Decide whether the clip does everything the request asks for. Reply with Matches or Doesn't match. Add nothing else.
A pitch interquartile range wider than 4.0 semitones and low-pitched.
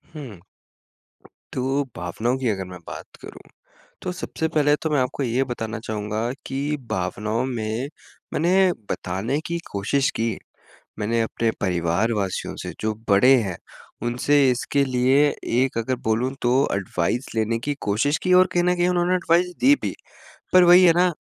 Matches